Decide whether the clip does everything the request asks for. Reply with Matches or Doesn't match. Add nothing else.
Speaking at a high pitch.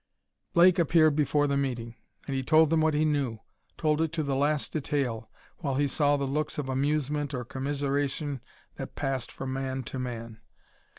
Doesn't match